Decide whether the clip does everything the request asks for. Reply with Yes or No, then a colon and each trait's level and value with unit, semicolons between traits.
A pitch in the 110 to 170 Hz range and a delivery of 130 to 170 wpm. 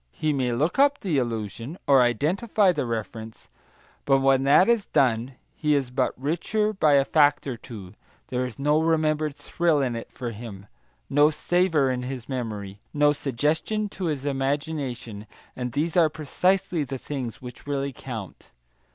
Yes: medium, 140 Hz; average, 165 wpm